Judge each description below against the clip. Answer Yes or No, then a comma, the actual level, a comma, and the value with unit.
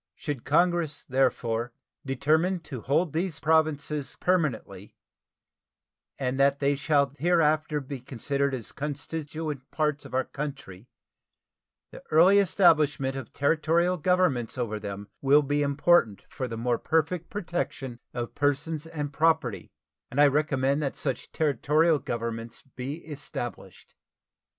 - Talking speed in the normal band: No, slow, 125 wpm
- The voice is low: No, medium, 145 Hz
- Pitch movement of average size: Yes, average, 3.5 semitones